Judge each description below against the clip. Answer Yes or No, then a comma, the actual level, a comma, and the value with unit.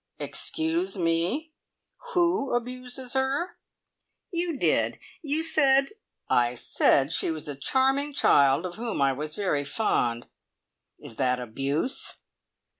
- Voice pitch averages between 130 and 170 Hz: No, high, 240 Hz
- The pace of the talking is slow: Yes, slow, 120 wpm